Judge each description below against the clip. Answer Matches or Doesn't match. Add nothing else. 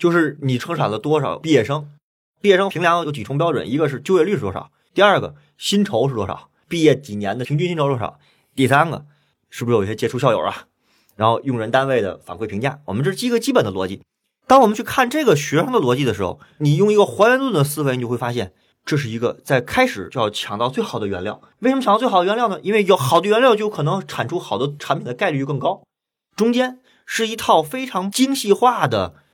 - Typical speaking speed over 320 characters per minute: Matches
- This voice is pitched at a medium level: Matches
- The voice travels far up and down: Matches